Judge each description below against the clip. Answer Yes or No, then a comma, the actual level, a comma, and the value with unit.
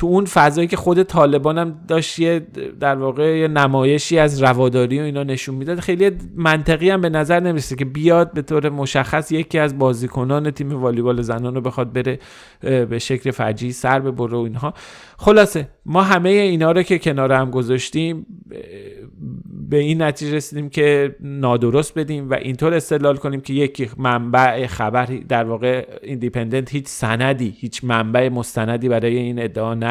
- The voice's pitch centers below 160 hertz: Yes, medium, 140 Hz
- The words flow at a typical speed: No, fast, 165 wpm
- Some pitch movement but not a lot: Yes, average, 3.9 semitones